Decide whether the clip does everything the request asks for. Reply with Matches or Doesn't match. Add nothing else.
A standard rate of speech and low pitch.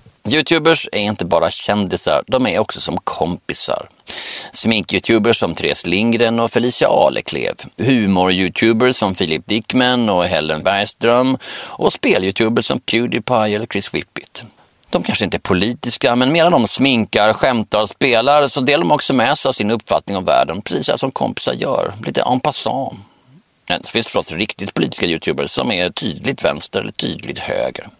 Matches